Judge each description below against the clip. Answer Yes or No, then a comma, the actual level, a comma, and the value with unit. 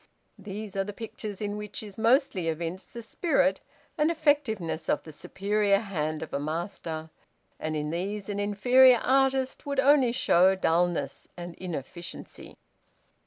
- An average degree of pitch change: No, wide, 5.9 semitones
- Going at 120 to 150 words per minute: Yes, average, 145 wpm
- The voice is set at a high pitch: Yes, high, 200 Hz